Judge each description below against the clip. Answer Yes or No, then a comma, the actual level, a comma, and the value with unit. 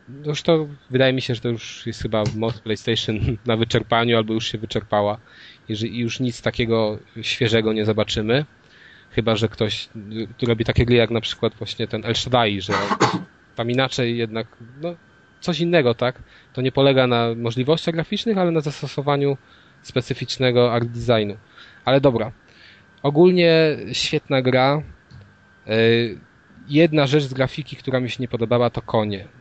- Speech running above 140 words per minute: Yes, average, 155 wpm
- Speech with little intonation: No, average, 3.2 semitones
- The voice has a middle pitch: No, low, 120 Hz